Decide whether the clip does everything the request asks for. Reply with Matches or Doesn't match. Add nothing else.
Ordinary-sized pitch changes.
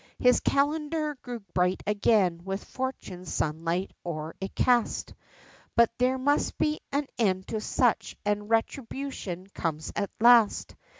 Doesn't match